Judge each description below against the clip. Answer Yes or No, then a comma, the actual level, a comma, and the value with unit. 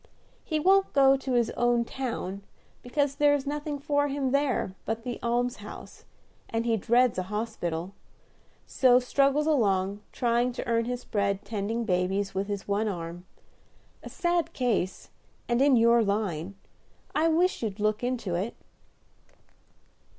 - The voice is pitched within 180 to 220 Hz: No, high, 235 Hz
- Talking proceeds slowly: No, average, 145 wpm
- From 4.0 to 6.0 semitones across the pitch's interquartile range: Yes, average, 5.2 semitones